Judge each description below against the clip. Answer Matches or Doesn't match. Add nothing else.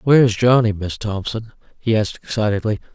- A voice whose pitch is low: Matches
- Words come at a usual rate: Matches